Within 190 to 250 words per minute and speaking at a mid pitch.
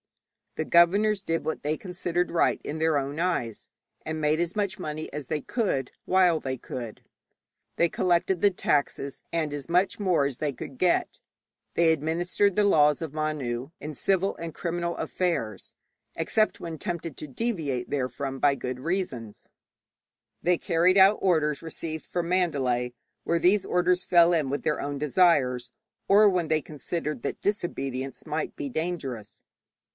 No: average, 160 wpm; medium, 160 Hz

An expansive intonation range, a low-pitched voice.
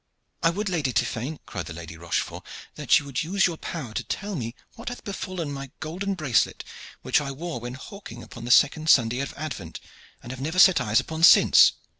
No: wide, 6.4 semitones; medium, 145 Hz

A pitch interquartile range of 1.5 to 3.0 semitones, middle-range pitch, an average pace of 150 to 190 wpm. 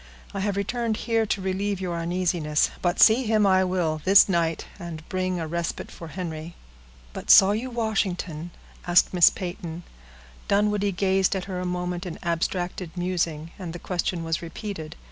Yes: average, 2.7 semitones; medium, 180 Hz; average, 165 wpm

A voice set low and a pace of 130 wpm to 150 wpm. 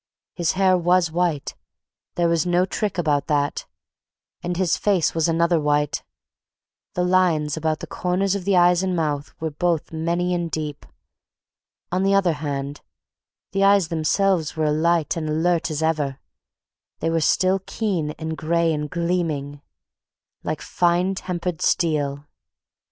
No: medium, 170 Hz; average, 145 wpm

